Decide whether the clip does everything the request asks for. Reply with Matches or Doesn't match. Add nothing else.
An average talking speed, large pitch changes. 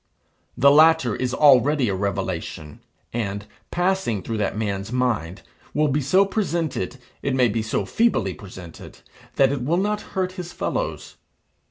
Matches